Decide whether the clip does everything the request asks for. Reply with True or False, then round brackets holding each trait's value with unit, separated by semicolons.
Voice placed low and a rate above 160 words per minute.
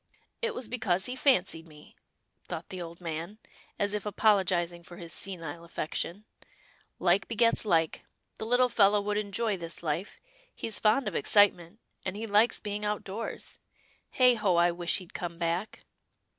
False (195 Hz; 170 wpm)